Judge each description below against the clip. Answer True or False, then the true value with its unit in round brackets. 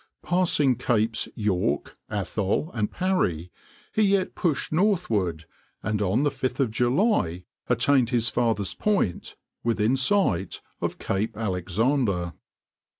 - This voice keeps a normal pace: False (105 wpm)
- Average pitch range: False (6.8 semitones)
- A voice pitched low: True (115 Hz)